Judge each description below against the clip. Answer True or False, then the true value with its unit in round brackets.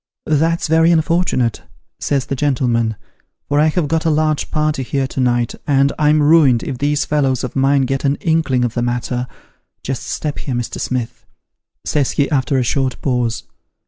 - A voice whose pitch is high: False (140 Hz)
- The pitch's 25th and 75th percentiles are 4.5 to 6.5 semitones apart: False (3.4 semitones)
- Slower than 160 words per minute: False (185 wpm)